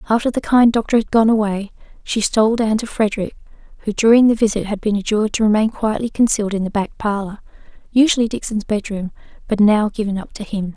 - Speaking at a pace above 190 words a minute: Yes, average, 200 wpm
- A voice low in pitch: No, high, 215 Hz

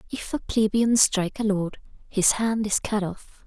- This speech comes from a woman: Yes, female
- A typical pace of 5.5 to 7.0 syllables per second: No, 4.4 syllables/s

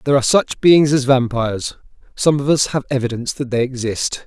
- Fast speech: No, average, 195 wpm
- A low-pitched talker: Yes, low, 130 Hz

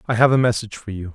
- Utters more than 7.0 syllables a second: Yes, 7.8 syllables/s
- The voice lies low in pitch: Yes, low, 110 Hz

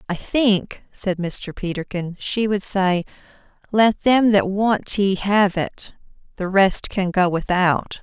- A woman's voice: Yes, female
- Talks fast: No, average, 150 wpm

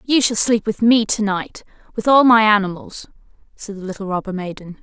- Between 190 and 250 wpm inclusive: Yes, average, 200 wpm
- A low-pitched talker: No, high, 210 Hz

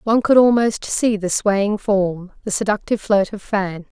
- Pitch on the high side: Yes, high, 205 Hz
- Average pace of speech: Yes, average, 180 wpm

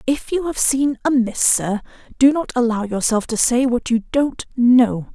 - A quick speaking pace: No, average, 185 wpm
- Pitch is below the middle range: No, high, 245 Hz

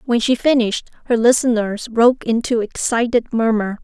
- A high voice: Yes, high, 230 Hz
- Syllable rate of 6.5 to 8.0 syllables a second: No, 5.2 syllables/s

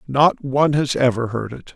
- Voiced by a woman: No, male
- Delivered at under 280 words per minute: Yes, fast, 205 wpm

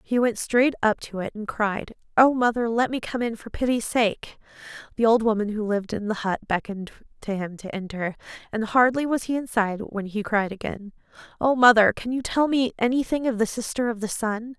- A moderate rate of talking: No, fast, 215 wpm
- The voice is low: No, high, 225 Hz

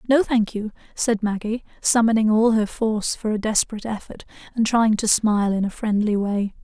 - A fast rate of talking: No, average, 190 wpm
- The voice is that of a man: No, female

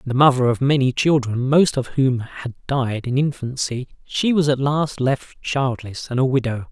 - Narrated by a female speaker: No, male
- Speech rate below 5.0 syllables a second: Yes, 4.6 syllables/s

